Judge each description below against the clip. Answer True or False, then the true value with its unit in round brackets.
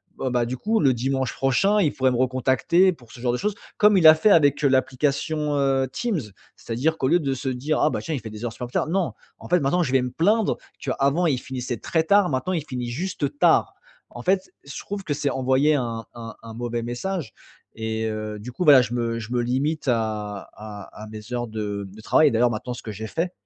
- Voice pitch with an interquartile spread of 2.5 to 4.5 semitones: False (4.9 semitones)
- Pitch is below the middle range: True (130 Hz)